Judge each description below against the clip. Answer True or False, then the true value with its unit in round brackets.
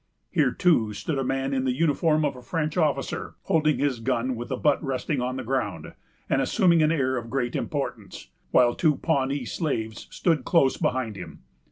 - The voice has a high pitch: False (135 Hz)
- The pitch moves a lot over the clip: False (3.7 semitones)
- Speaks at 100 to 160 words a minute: False (190 wpm)